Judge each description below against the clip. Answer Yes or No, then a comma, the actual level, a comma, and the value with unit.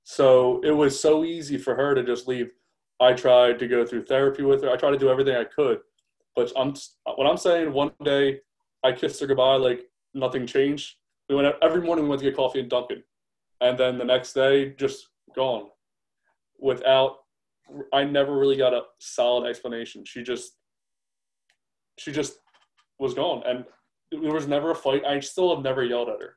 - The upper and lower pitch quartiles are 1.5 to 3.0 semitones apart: Yes, narrow, 2.5 semitones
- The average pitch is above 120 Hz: Yes, low, 135 Hz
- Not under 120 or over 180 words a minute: No, average, 190 wpm